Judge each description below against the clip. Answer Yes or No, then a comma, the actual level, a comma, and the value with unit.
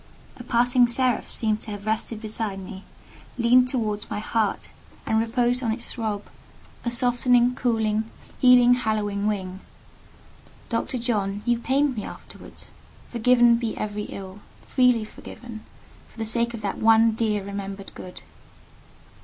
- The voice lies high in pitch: Yes, high, 225 Hz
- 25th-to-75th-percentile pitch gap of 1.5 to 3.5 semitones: Yes, narrow, 2.5 semitones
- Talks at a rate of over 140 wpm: No, slow, 135 wpm